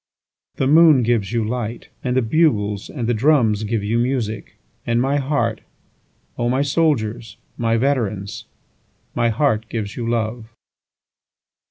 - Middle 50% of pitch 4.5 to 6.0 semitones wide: No, average, 3.3 semitones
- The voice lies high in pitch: No, low, 115 Hz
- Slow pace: Yes, slow, 125 wpm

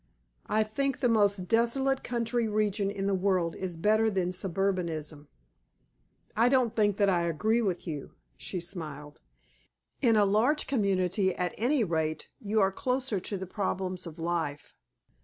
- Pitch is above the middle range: Yes, high, 195 Hz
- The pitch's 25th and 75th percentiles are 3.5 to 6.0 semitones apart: Yes, average, 4.0 semitones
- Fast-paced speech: No, average, 155 wpm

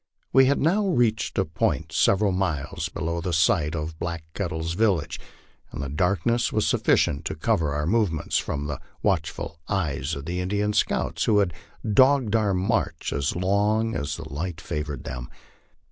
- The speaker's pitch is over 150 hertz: No, very low, 90 Hz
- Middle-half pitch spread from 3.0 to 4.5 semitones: No, average, 5.2 semitones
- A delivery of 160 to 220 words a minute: Yes, average, 165 wpm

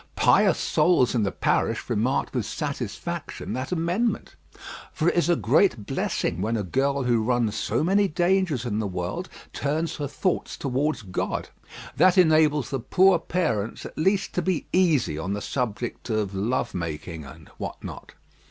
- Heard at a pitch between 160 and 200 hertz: No, low, 135 Hz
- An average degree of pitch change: No, wide, 8.3 semitones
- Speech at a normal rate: Yes, average, 165 wpm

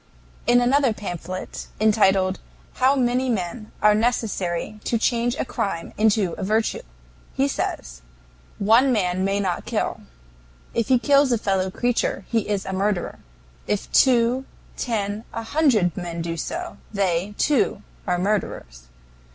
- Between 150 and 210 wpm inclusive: No, average, 140 wpm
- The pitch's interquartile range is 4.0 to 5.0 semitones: Yes, average, 4.5 semitones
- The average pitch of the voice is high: Yes, high, 210 Hz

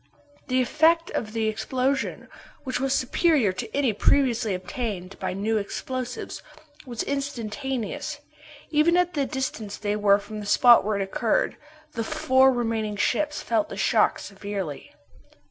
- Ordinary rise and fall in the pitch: Yes, average, 4.5 semitones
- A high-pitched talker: Yes, high, 235 Hz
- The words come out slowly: No, average, 145 wpm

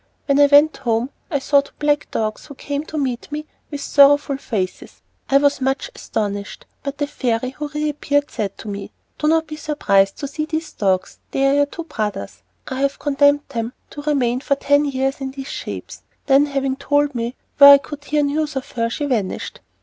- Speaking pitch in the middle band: No, very high, 280 Hz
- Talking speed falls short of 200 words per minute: No, fast, 205 wpm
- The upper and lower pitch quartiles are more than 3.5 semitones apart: No, average, 2.9 semitones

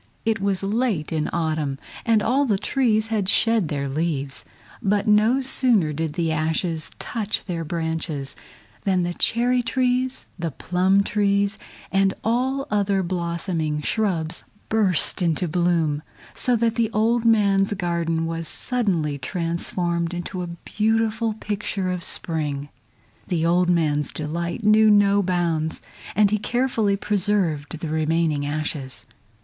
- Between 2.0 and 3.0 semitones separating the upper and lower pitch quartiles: No, average, 4.7 semitones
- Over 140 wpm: No, slow, 135 wpm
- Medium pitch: Yes, medium, 180 Hz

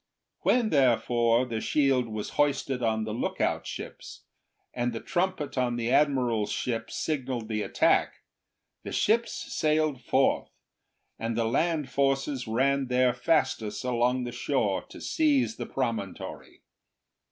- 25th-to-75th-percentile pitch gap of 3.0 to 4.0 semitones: Yes, average, 3.6 semitones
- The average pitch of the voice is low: Yes, low, 125 Hz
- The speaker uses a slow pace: Yes, slow, 130 wpm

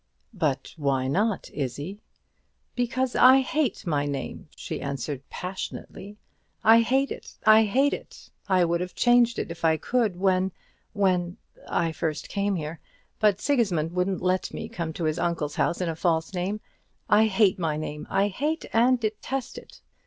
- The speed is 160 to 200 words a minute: Yes, average, 165 wpm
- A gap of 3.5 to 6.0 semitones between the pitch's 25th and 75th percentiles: Yes, wide, 5.5 semitones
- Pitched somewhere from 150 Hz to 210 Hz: Yes, medium, 185 Hz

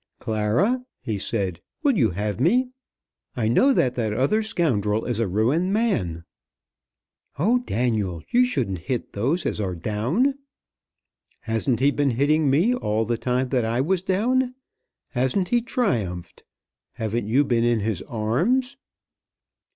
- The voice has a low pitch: Yes, low, 125 Hz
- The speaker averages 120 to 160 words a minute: Yes, average, 145 wpm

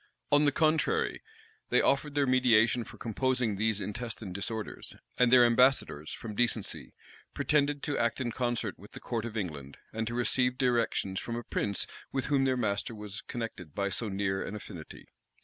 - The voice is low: Yes, low, 115 Hz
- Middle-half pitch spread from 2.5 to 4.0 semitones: Yes, average, 3.6 semitones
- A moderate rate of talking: Yes, average, 175 wpm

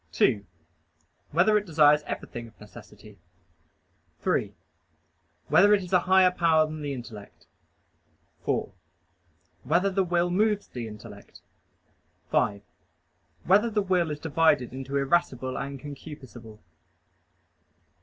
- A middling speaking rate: No, slow, 115 wpm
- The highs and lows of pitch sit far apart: Yes, wide, 6.4 semitones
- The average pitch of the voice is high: No, medium, 155 Hz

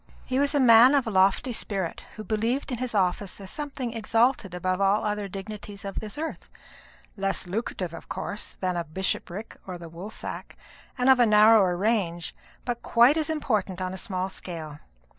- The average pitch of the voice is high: Yes, high, 210 Hz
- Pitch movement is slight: No, average, 4.2 semitones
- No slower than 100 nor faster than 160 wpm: No, average, 180 wpm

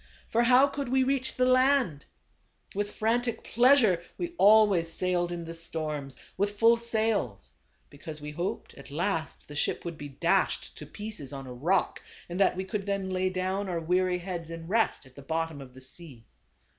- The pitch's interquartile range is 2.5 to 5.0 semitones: No, wide, 5.5 semitones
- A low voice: No, medium, 185 Hz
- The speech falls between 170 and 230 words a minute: Yes, average, 190 wpm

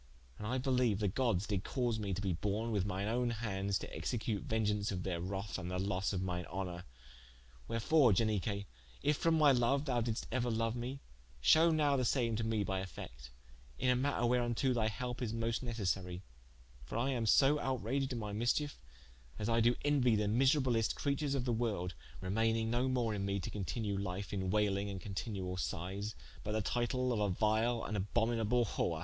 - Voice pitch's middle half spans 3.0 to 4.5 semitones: Yes, average, 3.8 semitones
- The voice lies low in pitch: Yes, low, 110 Hz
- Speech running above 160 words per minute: Yes, average, 195 wpm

